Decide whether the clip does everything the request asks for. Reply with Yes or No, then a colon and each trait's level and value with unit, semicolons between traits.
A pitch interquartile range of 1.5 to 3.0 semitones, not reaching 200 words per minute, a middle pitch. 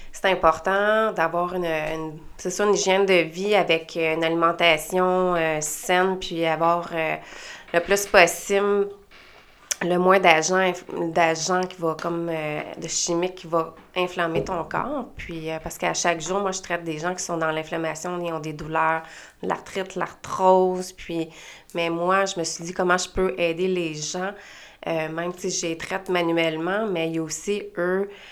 Yes: narrow, 2.4 semitones; average, 180 wpm; medium, 175 Hz